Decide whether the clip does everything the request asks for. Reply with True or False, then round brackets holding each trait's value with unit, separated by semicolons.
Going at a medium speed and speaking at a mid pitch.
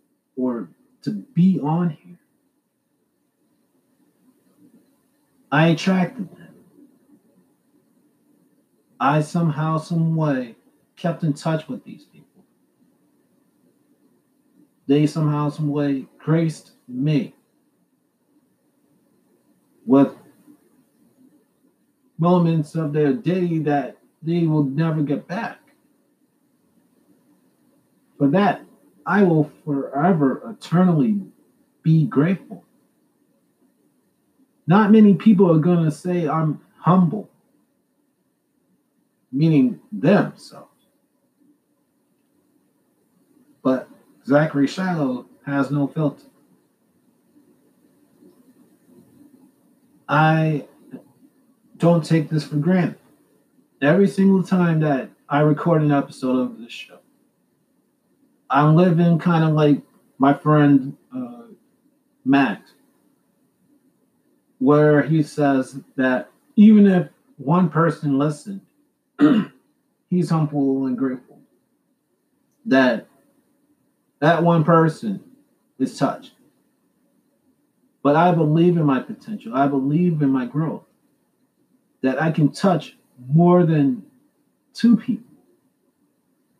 False (85 wpm; 175 Hz)